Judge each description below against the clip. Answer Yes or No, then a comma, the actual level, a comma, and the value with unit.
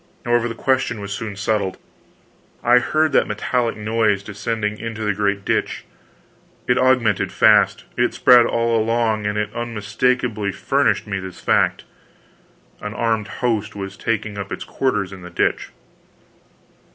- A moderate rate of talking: Yes, average, 145 wpm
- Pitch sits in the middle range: No, low, 110 Hz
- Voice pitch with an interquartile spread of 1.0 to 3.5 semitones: Yes, narrow, 2.5 semitones